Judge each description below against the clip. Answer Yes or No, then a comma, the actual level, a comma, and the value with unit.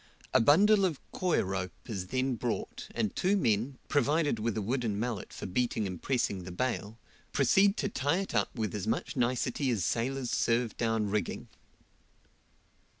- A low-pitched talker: Yes, low, 120 Hz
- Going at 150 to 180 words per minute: Yes, average, 165 wpm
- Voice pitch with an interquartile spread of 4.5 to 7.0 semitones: Yes, average, 5.0 semitones